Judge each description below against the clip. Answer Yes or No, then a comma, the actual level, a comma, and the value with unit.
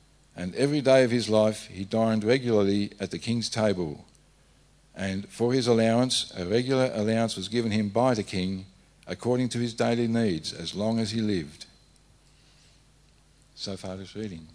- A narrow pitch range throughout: No, average, 3.3 semitones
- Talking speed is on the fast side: No, average, 165 wpm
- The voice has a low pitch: Yes, low, 110 Hz